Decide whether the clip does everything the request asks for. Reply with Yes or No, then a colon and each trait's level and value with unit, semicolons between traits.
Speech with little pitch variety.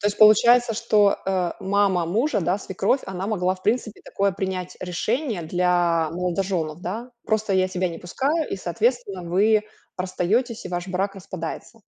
No: average, 3.2 semitones